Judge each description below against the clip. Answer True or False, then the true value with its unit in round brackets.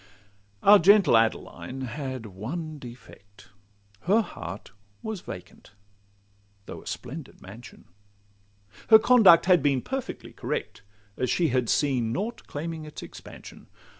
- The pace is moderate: False (120 wpm)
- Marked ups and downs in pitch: True (7.3 semitones)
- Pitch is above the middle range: False (140 Hz)